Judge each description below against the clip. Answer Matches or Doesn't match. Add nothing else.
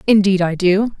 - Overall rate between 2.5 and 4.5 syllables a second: Doesn't match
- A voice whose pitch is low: Doesn't match